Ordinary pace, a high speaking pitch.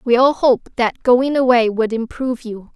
Yes: average, 195 wpm; high, 240 Hz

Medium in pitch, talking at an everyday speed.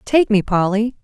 No: high, 215 Hz; average, 175 wpm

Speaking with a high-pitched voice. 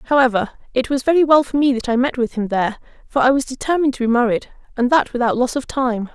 Yes: very high, 255 Hz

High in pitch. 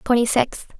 Yes: high, 240 Hz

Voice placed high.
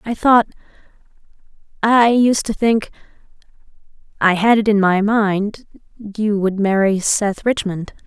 Yes: high, 210 Hz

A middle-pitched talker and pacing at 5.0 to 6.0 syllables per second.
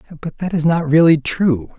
Yes: medium, 155 Hz; 5.1 syllables/s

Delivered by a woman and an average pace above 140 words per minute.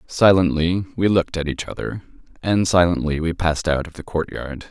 No: male; average, 180 wpm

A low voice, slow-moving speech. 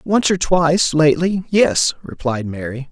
No: medium, 155 Hz; slow, 125 wpm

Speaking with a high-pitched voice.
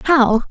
Yes: very high, 255 Hz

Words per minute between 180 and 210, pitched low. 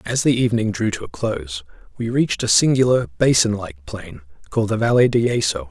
Yes: average, 200 wpm; low, 120 Hz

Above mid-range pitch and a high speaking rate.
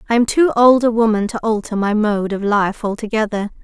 Yes: high, 220 Hz; fast, 215 wpm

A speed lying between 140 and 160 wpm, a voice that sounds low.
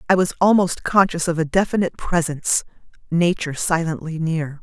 No: average, 145 wpm; medium, 170 Hz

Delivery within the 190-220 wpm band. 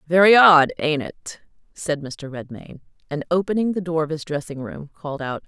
No: average, 175 wpm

